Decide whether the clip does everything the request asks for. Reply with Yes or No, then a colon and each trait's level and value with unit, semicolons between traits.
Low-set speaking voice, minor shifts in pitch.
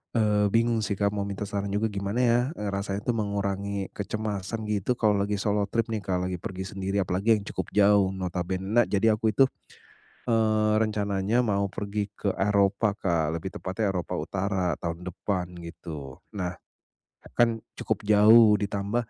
Yes: low, 100 Hz; narrow, 2.0 semitones